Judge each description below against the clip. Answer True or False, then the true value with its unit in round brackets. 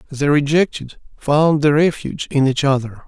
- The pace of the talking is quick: False (155 wpm)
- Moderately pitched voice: True (145 Hz)